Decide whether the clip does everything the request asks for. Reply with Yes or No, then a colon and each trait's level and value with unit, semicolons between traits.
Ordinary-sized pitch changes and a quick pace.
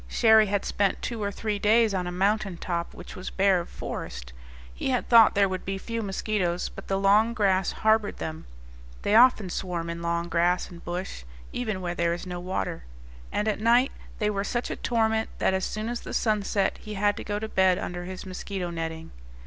Yes: average, 3.3 semitones; fast, 215 wpm